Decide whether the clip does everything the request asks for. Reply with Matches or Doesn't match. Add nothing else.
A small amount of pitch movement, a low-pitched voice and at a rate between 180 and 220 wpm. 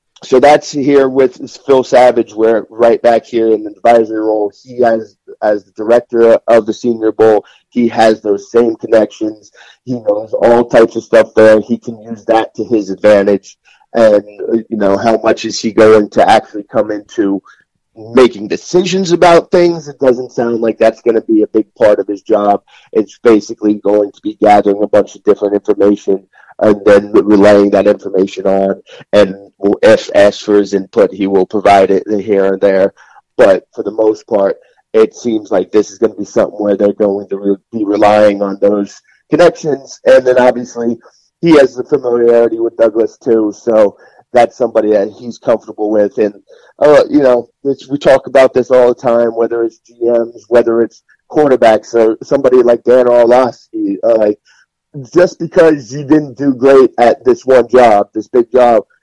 Doesn't match